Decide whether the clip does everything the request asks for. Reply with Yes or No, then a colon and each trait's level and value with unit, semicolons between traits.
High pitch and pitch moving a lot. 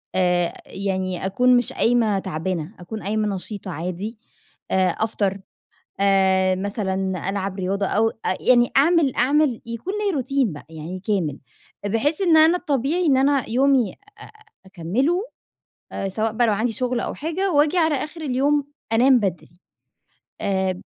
Yes: high, 220 Hz; wide, 6.3 semitones